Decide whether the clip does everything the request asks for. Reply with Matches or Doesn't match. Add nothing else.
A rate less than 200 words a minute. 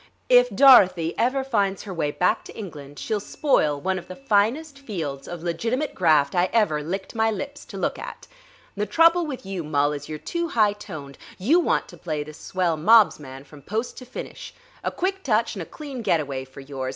Doesn't match